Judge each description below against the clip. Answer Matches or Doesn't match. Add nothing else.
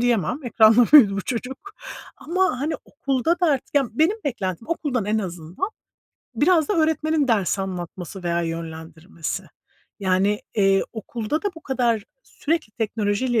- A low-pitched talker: Doesn't match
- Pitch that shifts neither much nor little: Doesn't match